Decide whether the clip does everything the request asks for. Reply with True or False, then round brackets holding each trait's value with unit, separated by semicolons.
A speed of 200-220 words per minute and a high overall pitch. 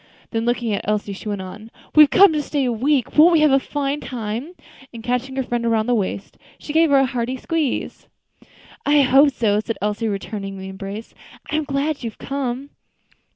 True (205 wpm; 245 Hz)